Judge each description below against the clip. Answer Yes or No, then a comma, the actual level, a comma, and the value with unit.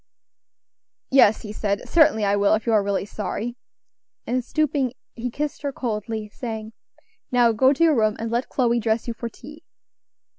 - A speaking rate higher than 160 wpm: Yes, average, 175 wpm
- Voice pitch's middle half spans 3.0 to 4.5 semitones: Yes, average, 3.3 semitones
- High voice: Yes, high, 230 Hz